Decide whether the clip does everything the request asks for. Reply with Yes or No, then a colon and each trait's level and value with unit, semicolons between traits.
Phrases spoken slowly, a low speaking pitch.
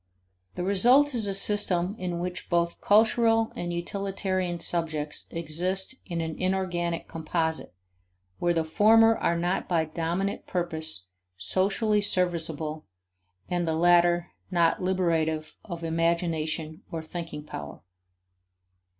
No: slow, 115 wpm; medium, 175 Hz